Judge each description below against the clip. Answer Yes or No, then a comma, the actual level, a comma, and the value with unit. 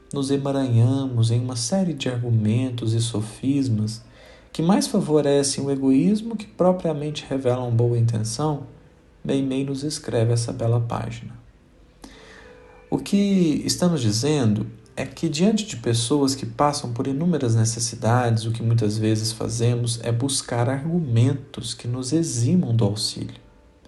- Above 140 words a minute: No, average, 130 wpm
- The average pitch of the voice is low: Yes, low, 125 Hz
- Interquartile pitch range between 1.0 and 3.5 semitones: No, average, 4.2 semitones